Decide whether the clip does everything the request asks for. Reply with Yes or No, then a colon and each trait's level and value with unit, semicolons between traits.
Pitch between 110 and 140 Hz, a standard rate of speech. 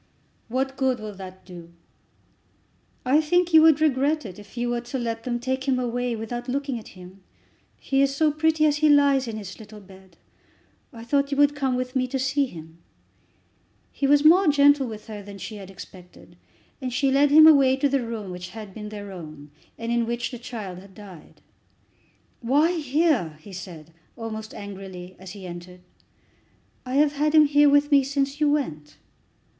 No: high, 245 Hz; average, 190 wpm